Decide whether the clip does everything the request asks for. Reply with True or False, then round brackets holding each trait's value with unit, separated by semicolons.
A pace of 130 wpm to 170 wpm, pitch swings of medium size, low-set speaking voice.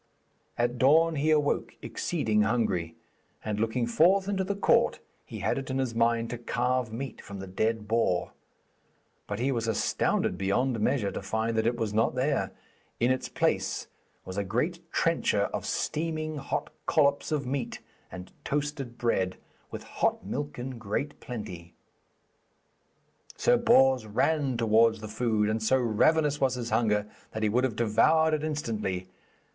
True (160 wpm; 4.6 semitones; 120 Hz)